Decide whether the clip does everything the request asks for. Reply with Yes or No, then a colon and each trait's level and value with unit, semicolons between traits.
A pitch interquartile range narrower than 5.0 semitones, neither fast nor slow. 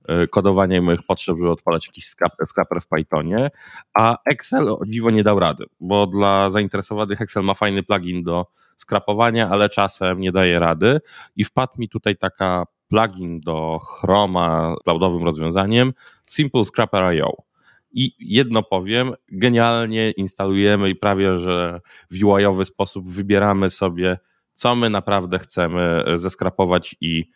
Yes: narrow, 2.6 semitones; average, 140 wpm